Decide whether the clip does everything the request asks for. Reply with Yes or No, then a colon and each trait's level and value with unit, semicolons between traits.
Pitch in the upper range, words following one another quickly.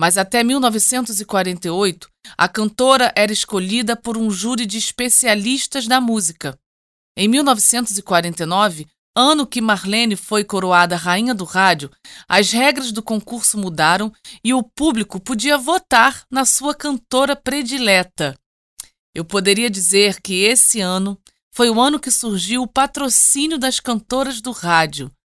No: high, 220 Hz; average, 130 wpm